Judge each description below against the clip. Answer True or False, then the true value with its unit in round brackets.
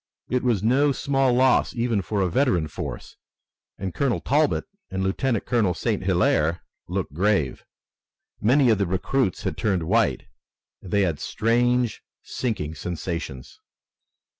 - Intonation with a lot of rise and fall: True (5.7 semitones)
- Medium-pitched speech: False (105 Hz)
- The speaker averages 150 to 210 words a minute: False (140 wpm)